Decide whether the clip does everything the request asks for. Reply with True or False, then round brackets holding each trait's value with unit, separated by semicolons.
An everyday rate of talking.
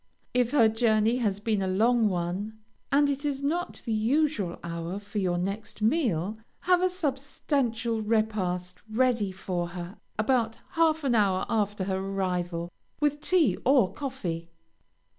True (145 wpm)